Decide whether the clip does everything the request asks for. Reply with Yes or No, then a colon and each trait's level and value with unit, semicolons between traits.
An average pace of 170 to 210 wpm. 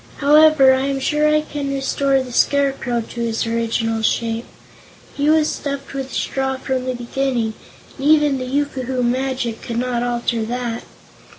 No: average, 160 wpm